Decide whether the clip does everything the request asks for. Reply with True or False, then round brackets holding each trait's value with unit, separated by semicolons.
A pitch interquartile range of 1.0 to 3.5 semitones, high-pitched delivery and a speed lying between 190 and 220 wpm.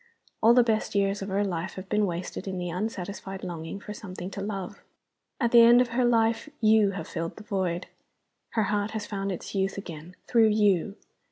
True (2.9 semitones; 200 Hz; 200 wpm)